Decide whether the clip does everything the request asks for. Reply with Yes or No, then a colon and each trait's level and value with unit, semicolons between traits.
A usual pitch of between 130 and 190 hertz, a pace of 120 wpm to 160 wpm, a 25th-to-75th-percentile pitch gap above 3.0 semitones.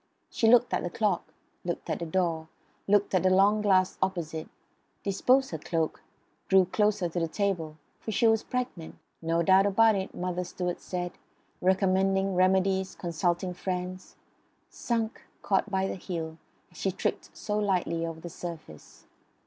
No: medium, 185 Hz; average, 155 wpm; narrow, 2.5 semitones